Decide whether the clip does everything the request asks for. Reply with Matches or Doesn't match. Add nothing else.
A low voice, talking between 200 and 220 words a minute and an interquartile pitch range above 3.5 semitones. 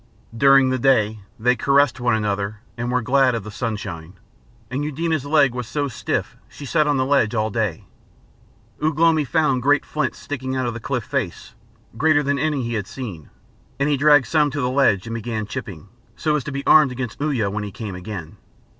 Matches